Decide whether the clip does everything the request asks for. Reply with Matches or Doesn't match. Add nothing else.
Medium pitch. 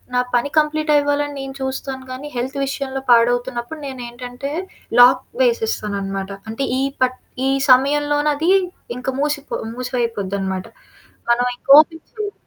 Doesn't match